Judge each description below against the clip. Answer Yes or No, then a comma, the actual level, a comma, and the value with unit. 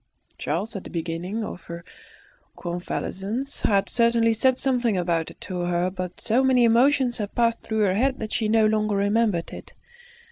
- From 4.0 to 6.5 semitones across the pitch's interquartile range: Yes, average, 4.3 semitones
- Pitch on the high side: Yes, high, 215 Hz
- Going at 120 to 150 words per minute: No, average, 175 wpm